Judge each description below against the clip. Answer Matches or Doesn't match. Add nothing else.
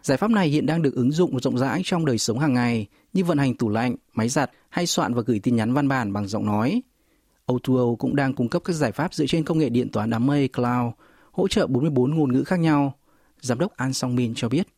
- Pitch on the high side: Doesn't match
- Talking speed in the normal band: Doesn't match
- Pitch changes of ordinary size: Matches